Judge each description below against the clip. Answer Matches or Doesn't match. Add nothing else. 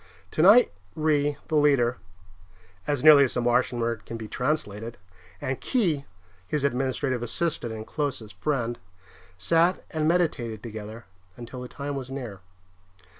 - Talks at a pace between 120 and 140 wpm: Matches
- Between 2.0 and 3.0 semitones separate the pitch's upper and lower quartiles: Doesn't match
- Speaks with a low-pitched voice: Matches